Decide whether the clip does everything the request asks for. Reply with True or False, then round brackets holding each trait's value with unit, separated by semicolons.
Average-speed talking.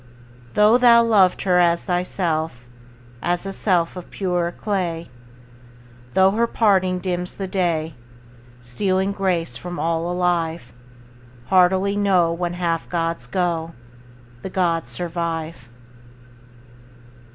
False (110 wpm)